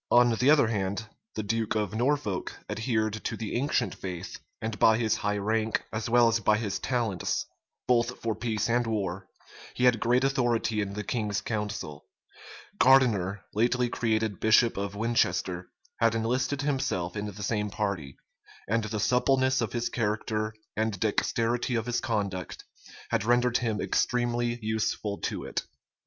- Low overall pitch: Yes, low, 110 Hz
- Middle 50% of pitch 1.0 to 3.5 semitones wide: Yes, narrow, 2.6 semitones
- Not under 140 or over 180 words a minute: Yes, average, 155 wpm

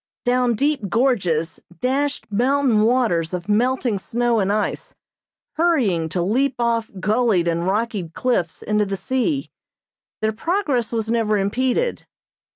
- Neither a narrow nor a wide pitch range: Yes, average, 4.5 semitones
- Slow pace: Yes, slow, 130 wpm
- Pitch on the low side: No, high, 230 Hz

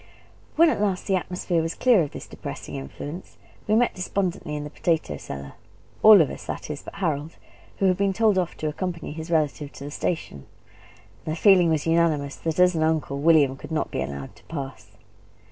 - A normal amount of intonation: Yes, average, 3.9 semitones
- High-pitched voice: No, medium, 165 Hz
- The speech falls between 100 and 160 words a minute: No, fast, 205 wpm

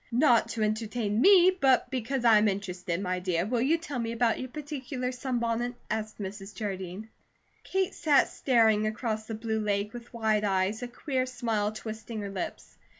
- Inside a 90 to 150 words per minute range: No, average, 175 wpm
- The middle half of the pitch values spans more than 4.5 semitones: No, average, 3.2 semitones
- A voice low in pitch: No, high, 225 Hz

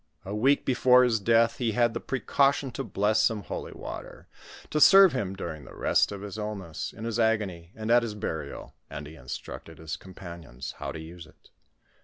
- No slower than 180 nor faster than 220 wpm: Yes, average, 200 wpm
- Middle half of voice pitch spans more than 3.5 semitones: Yes, wide, 5.6 semitones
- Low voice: Yes, low, 105 Hz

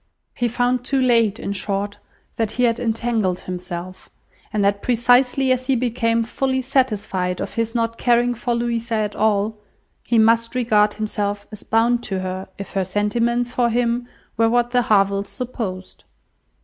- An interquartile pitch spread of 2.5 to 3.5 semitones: Yes, average, 3.0 semitones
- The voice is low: No, high, 230 Hz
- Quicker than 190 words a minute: No, average, 160 wpm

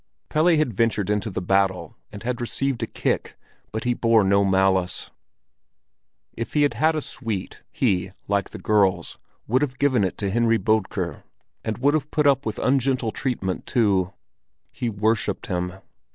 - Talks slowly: No, average, 165 wpm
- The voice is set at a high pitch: No, low, 110 Hz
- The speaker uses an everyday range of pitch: Yes, average, 4.9 semitones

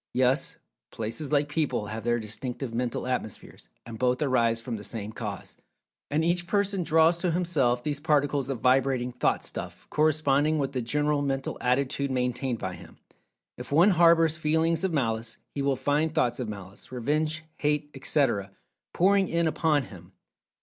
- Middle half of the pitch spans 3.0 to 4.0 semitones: No, average, 4.6 semitones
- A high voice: No, low, 135 Hz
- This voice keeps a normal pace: Yes, average, 165 wpm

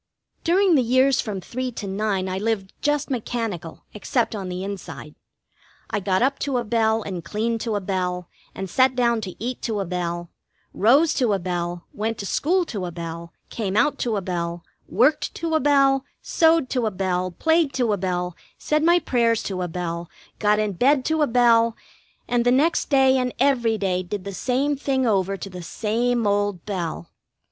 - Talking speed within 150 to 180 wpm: No, average, 195 wpm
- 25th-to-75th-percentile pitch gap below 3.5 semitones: No, wide, 5.6 semitones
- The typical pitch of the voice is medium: No, high, 220 Hz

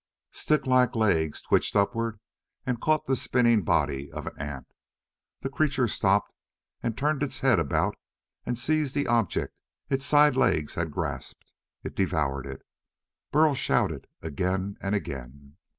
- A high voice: No, low, 110 Hz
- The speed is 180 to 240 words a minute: No, average, 140 wpm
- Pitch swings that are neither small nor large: No, wide, 8.8 semitones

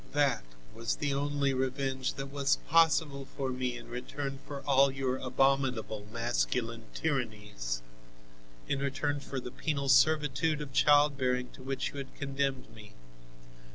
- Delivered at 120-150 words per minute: Yes, average, 140 wpm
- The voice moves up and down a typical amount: No, narrow, 2.0 semitones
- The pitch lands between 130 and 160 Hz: Yes, low, 135 Hz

